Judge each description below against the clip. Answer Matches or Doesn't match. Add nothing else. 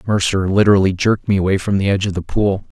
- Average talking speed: Doesn't match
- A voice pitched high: Doesn't match